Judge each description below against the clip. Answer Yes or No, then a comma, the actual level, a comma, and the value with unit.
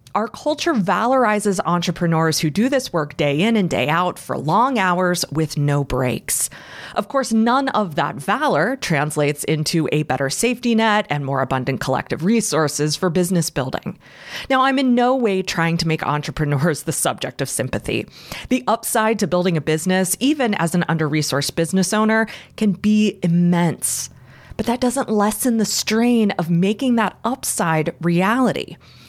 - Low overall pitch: No, medium, 180 Hz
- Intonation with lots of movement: Yes, wide, 6.1 semitones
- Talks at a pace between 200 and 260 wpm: No, average, 165 wpm